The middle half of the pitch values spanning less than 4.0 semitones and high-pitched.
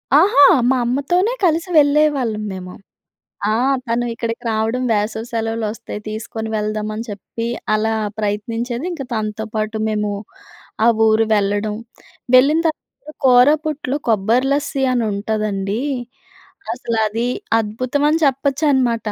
No: average, 4.3 semitones; high, 230 Hz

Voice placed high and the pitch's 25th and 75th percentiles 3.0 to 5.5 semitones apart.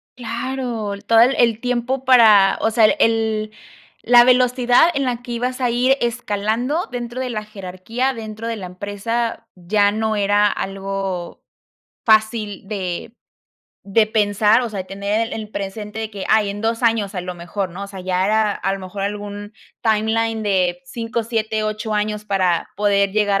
No: high, 215 Hz; narrow, 2.6 semitones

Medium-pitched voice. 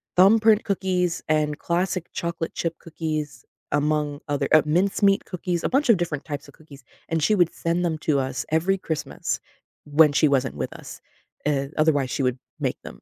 Yes: medium, 160 Hz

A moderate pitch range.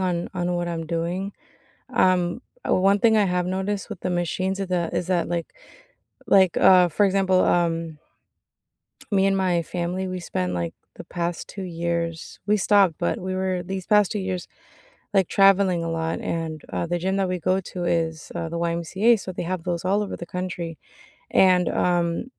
No: narrow, 2.0 semitones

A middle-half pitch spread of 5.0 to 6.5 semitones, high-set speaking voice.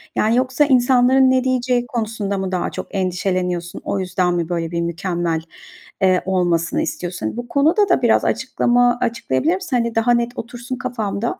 Yes: wide, 5.5 semitones; high, 230 Hz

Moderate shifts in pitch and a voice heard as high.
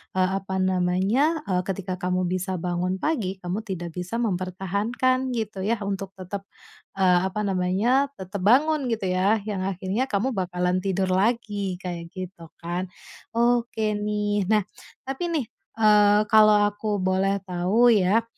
Yes: average, 3.0 semitones; high, 195 Hz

